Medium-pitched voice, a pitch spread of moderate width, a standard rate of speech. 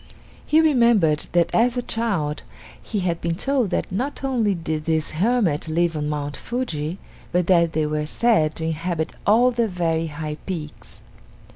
No: medium, 170 Hz; wide, 6.7 semitones; average, 165 wpm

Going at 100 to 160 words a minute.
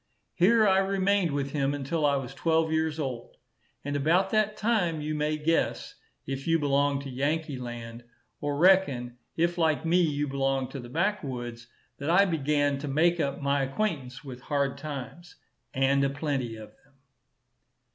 No: average, 170 wpm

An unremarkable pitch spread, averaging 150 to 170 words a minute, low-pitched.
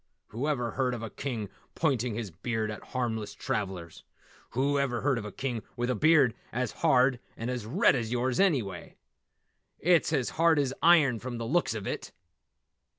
Yes: average, 3.7 semitones; average, 160 wpm; low, 125 Hz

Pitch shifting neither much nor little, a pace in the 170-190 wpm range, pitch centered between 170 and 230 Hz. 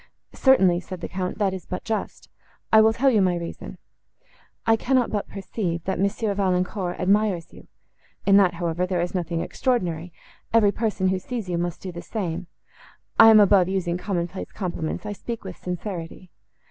Yes: average, 3.1 semitones; average, 180 wpm; medium, 185 Hz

